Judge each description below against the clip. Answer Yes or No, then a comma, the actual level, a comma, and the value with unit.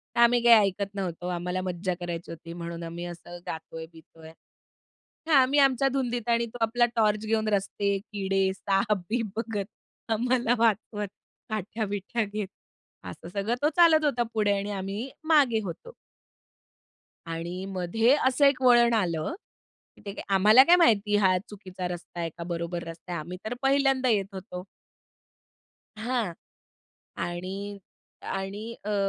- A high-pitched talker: Yes, high, 205 Hz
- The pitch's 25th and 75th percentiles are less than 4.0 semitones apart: No, average, 4.7 semitones